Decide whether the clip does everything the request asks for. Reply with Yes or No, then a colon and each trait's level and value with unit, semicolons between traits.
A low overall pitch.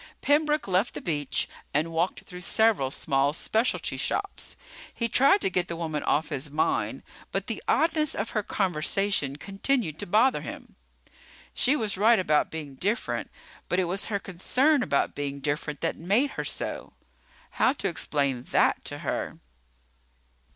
No: medium, 185 Hz